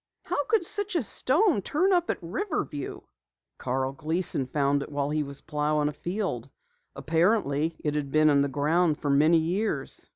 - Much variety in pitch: Yes, wide, 6.5 semitones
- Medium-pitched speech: Yes, medium, 155 Hz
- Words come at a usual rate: Yes, average, 170 wpm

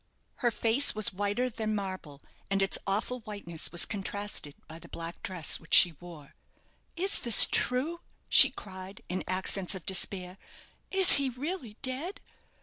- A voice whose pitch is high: Yes, high, 200 Hz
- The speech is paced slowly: No, average, 150 wpm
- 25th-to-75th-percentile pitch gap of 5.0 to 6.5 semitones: Yes, wide, 5.4 semitones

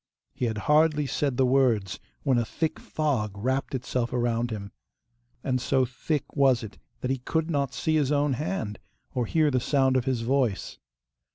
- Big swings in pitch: No, average, 3.3 semitones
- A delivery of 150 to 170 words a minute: No, average, 180 wpm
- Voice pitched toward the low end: Yes, low, 130 Hz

